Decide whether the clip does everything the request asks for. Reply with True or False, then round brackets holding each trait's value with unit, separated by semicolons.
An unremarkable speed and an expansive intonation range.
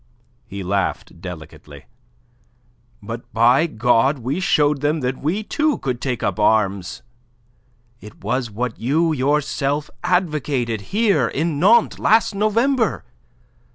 False (120 wpm; 6.9 semitones)